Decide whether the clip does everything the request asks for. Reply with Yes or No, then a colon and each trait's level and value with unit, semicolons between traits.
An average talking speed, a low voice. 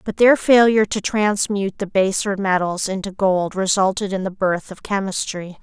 No: average, 170 wpm; high, 195 Hz